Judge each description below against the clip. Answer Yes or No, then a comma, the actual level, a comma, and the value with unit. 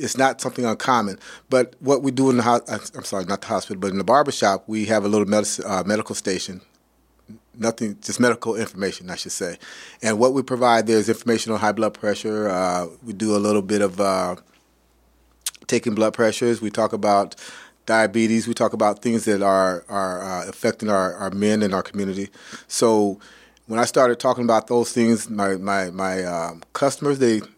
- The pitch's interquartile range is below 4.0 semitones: Yes, average, 2.9 semitones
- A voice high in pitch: No, low, 110 Hz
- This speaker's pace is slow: No, average, 195 wpm